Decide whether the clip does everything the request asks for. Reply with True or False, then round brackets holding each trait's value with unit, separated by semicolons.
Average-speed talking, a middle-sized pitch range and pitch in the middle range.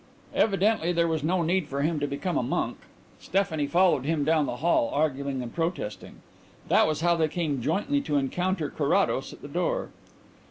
True (185 wpm; 4.0 semitones; 160 Hz)